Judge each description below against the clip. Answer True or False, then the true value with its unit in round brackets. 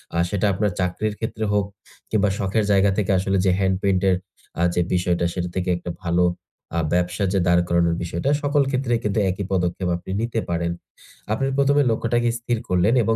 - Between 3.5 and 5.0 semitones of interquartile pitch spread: True (3.8 semitones)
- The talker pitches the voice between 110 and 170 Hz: False (95 Hz)